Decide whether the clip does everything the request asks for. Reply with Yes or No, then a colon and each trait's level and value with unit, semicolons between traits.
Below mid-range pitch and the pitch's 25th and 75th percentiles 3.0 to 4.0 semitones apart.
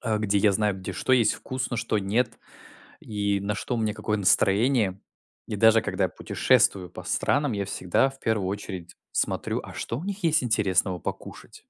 Yes: low, 105 Hz; average, 3.3 semitones